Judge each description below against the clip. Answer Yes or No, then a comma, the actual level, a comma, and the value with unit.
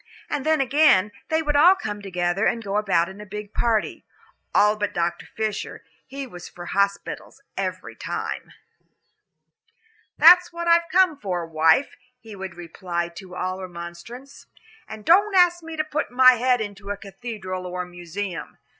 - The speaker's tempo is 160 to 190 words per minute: Yes, average, 165 wpm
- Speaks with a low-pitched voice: No, high, 210 Hz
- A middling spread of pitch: No, wide, 7.3 semitones